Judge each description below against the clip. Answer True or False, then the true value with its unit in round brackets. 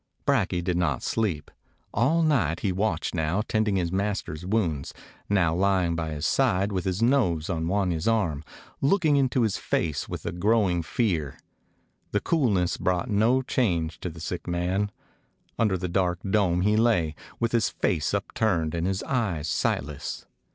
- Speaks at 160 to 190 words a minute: True (165 wpm)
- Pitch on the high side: False (95 Hz)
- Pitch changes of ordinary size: True (4.6 semitones)